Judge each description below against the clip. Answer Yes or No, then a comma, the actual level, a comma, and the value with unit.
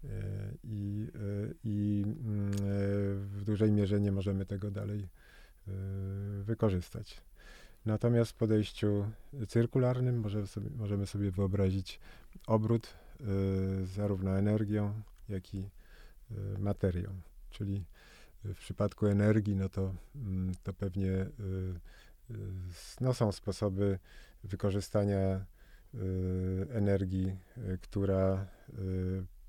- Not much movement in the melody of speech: Yes, narrow, 1.7 semitones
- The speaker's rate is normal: No, slow, 80 wpm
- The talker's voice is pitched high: No, low, 100 Hz